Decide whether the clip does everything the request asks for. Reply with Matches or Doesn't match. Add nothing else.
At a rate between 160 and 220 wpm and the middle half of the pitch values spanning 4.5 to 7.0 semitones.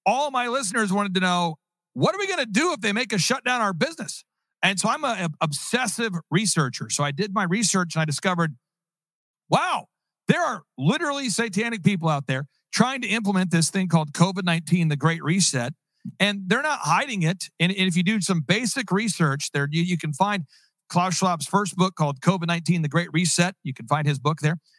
Doesn't match